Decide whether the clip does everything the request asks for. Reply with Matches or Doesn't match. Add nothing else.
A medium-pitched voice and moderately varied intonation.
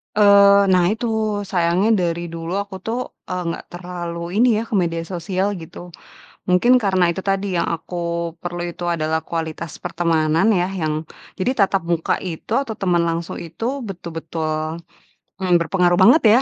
Matches